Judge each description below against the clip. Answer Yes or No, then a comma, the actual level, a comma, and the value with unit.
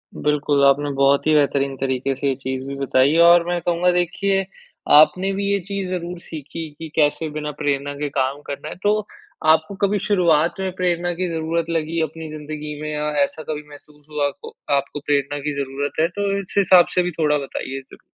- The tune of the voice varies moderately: Yes, average, 3.5 semitones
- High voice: No, medium, 155 Hz